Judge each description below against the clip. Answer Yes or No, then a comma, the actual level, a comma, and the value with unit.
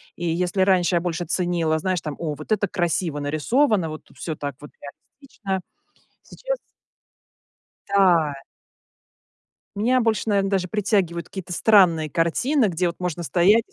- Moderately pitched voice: Yes, medium, 180 Hz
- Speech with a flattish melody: No, average, 3.6 semitones